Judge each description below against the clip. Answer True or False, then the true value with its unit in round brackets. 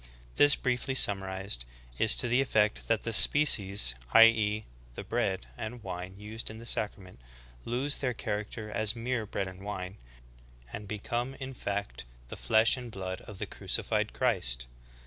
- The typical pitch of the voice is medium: False (105 Hz)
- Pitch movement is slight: False (3.4 semitones)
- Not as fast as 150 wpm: False (160 wpm)